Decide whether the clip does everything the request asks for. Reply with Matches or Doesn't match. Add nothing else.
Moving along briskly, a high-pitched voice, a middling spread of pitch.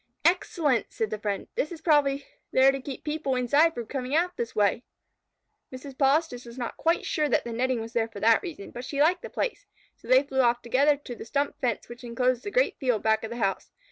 Matches